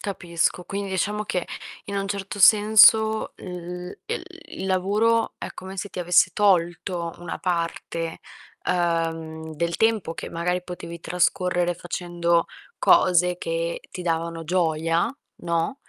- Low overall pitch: No, medium, 180 Hz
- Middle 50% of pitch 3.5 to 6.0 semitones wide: No, narrow, 2.5 semitones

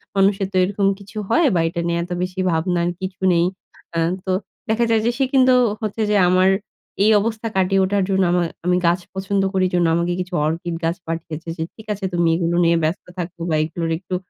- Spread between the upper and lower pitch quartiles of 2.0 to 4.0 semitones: Yes, narrow, 2.6 semitones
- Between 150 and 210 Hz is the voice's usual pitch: Yes, medium, 185 Hz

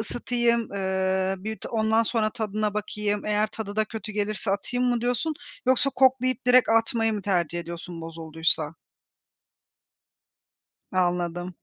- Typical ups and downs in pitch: Yes, average, 3.6 semitones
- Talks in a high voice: Yes, high, 210 Hz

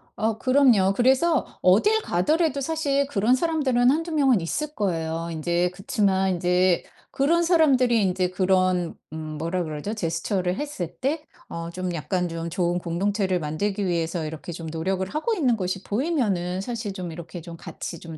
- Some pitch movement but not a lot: No, wide, 7.1 semitones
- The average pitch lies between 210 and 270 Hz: No, high, 190 Hz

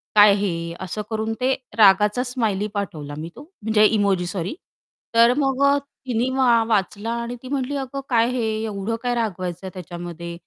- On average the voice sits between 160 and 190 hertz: No, high, 215 Hz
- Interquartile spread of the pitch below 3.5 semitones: No, average, 4.6 semitones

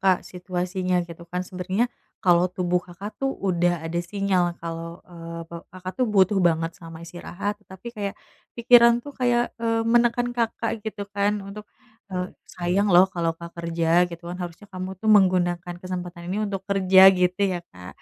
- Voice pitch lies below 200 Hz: Yes, medium, 185 Hz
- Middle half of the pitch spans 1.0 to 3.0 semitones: Yes, narrow, 2.6 semitones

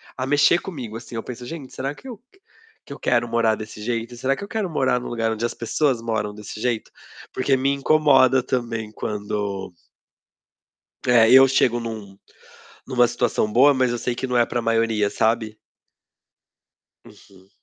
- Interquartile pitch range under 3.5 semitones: Yes, average, 3.0 semitones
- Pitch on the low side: Yes, low, 120 Hz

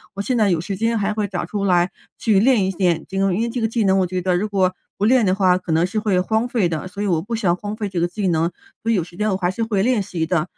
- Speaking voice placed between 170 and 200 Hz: Yes, high, 195 Hz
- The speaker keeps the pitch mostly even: No, average, 3.2 semitones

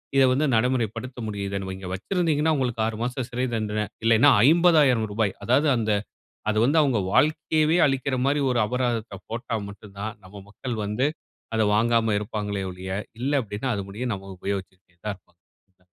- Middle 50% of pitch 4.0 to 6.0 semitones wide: Yes, average, 4.3 semitones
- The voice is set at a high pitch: No, low, 115 Hz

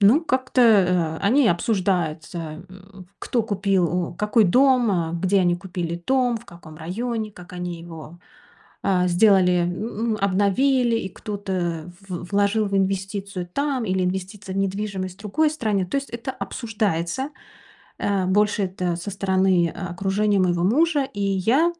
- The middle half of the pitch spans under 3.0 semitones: No, average, 3.6 semitones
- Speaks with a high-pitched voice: Yes, high, 195 Hz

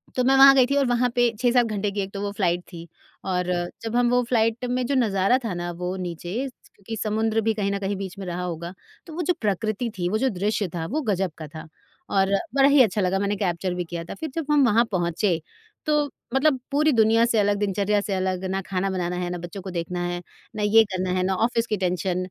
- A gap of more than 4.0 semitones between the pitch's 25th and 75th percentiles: Yes, average, 4.6 semitones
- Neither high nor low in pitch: No, high, 200 Hz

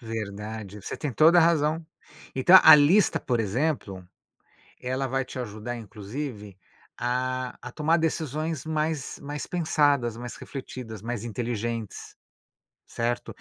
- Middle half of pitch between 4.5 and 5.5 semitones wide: Yes, average, 5.2 semitones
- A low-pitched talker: Yes, low, 125 Hz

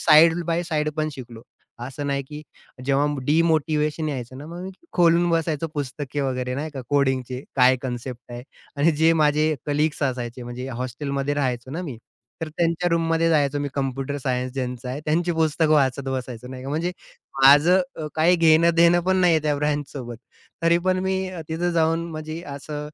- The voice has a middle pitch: Yes, medium, 150 Hz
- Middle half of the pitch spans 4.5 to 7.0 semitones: No, average, 3.7 semitones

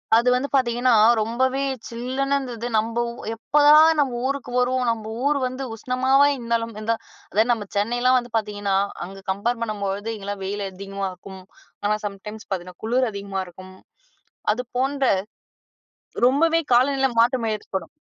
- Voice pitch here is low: No, high, 235 Hz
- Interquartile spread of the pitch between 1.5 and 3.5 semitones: No, average, 4.1 semitones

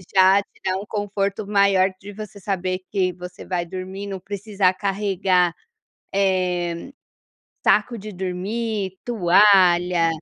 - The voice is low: No, high, 190 Hz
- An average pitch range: No, narrow, 1.8 semitones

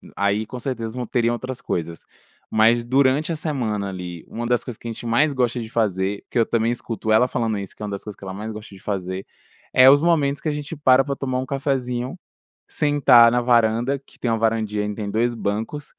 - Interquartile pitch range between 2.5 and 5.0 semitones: Yes, average, 3.5 semitones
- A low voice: Yes, low, 115 Hz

